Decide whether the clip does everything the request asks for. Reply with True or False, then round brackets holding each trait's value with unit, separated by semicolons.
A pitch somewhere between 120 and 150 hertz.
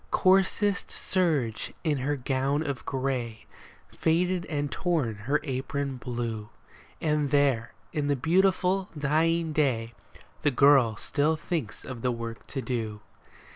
True (140 Hz)